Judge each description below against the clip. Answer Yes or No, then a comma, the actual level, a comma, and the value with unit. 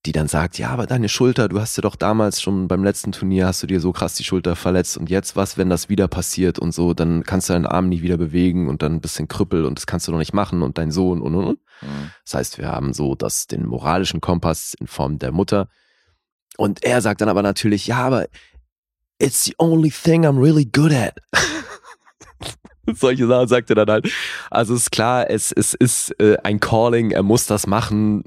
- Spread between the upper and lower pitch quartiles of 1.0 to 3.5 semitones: No, average, 4.3 semitones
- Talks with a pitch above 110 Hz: No, very low, 95 Hz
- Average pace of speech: No, fast, 230 wpm